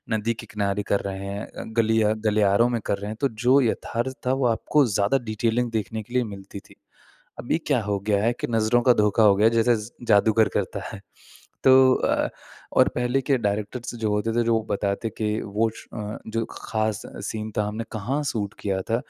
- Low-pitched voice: Yes, low, 110 Hz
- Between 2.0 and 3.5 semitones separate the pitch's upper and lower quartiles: Yes, narrow, 2.4 semitones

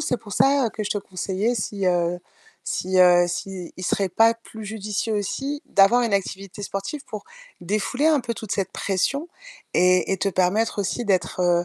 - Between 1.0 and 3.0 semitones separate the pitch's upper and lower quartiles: No, average, 3.5 semitones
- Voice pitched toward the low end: No, high, 200 Hz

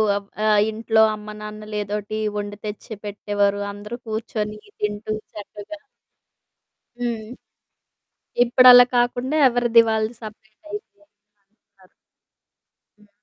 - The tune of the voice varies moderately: No, narrow, 2.2 semitones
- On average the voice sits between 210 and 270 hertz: Yes, high, 215 Hz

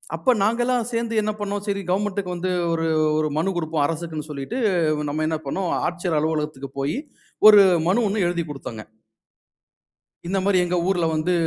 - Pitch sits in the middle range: Yes, medium, 175 Hz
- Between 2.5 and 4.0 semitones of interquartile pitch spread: No, average, 4.5 semitones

